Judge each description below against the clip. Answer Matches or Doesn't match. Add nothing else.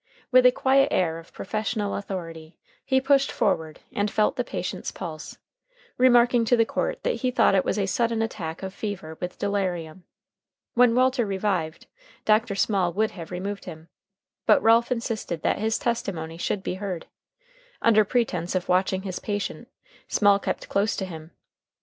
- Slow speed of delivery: Doesn't match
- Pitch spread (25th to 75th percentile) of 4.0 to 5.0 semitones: Matches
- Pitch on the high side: Matches